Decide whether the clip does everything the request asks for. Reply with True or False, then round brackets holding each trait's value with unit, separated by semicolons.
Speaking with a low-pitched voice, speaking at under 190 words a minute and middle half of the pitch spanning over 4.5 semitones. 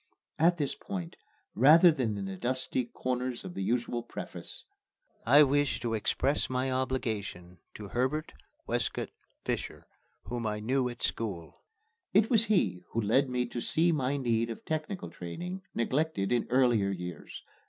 True (125 Hz; 155 wpm; 5.0 semitones)